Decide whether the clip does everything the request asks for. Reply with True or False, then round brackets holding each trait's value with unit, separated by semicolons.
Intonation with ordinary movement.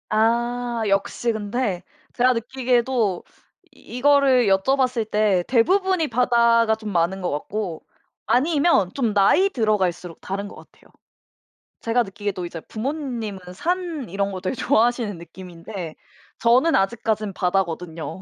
True (4.5 semitones)